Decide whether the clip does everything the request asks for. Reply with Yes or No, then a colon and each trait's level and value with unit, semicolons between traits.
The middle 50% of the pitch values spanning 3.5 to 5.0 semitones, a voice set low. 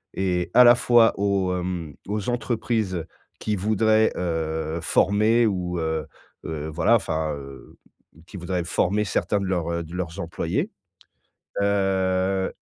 Yes: average, 3.8 semitones; very low, 95 Hz